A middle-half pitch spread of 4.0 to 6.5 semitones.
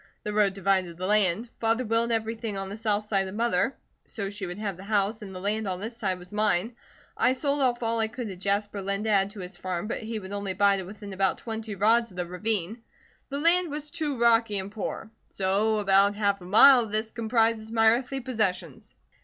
No: average, 2.8 semitones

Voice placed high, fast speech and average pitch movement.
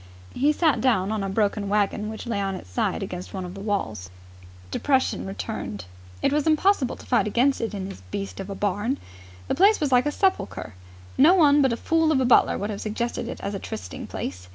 No: high, 220 Hz; fast, 225 wpm; wide, 5.9 semitones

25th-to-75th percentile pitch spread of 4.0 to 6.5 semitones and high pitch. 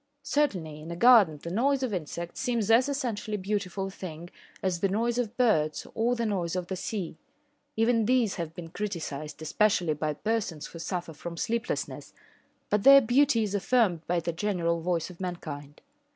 Yes: average, 5.2 semitones; high, 195 Hz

